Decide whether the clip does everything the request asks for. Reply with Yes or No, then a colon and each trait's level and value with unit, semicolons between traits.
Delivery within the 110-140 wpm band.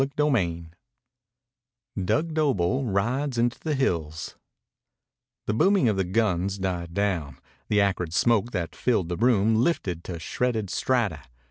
Yes: slow, 135 wpm